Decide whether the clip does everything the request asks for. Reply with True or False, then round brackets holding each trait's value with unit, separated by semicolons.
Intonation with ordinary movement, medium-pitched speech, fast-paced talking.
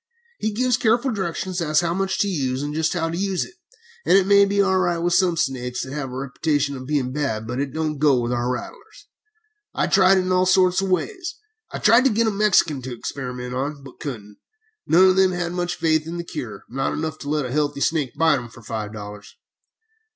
False (6.1 semitones; 160 Hz; 235 wpm)